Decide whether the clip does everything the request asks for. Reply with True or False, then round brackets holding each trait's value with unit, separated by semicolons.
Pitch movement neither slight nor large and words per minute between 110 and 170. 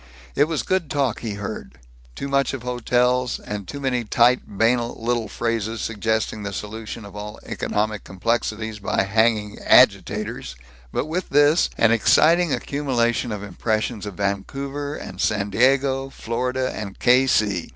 True (4.0 semitones; 150 wpm)